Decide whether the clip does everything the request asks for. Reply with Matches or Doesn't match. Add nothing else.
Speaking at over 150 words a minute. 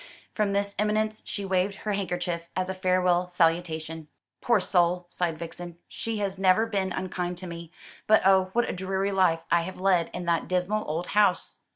Matches